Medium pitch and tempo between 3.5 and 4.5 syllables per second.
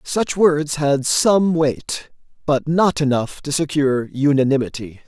Yes: medium, 145 Hz; 4.0 syllables/s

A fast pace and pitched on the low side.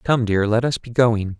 Yes: fast, 255 wpm; low, 115 Hz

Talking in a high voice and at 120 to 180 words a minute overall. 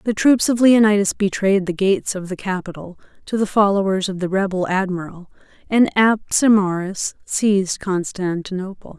Yes: high, 195 Hz; average, 140 wpm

